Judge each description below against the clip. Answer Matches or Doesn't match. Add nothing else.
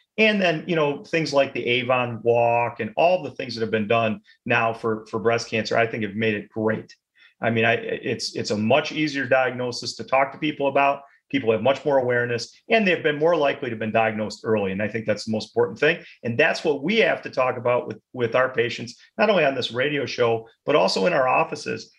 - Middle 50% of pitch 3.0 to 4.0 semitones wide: Matches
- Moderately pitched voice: Doesn't match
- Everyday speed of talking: Doesn't match